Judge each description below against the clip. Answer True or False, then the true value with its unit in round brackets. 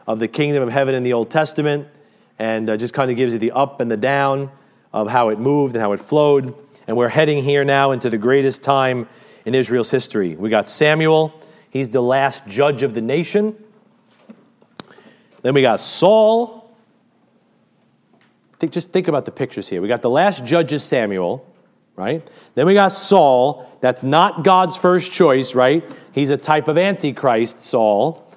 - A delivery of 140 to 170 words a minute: False (180 wpm)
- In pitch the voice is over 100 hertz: True (140 Hz)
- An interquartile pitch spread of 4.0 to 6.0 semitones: True (5.5 semitones)